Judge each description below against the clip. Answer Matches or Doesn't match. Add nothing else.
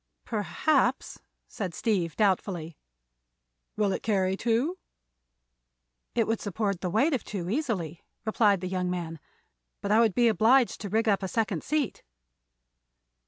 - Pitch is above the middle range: Matches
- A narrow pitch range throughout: Doesn't match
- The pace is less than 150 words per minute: Matches